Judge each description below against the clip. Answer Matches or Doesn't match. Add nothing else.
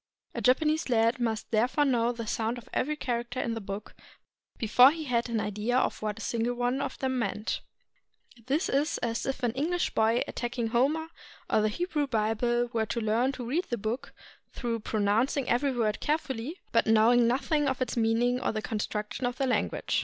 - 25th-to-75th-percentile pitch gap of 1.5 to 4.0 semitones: Matches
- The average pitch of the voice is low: Doesn't match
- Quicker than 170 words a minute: Matches